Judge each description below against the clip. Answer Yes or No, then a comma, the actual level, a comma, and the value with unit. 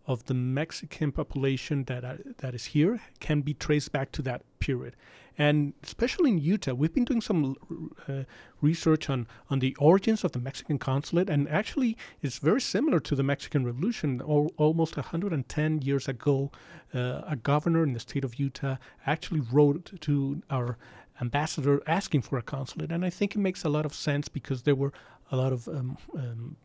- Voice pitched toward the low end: No, medium, 145 Hz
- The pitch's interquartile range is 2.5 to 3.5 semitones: Yes, average, 2.9 semitones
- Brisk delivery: No, average, 185 wpm